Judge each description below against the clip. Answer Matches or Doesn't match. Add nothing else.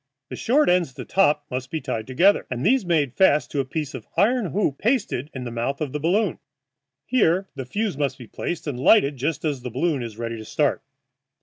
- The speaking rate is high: Matches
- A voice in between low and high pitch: Matches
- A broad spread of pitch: Matches